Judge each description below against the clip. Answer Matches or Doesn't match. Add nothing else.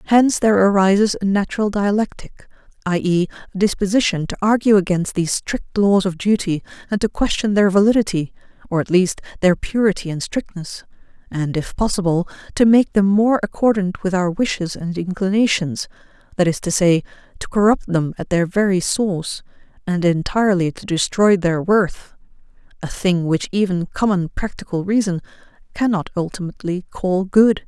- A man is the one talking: Doesn't match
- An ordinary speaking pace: Matches